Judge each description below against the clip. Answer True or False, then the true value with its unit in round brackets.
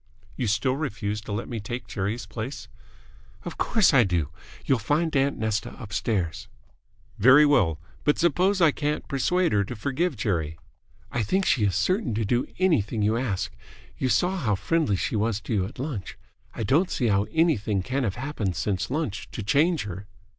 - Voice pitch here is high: False (120 Hz)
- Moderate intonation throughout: False (6.3 semitones)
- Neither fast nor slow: True (180 wpm)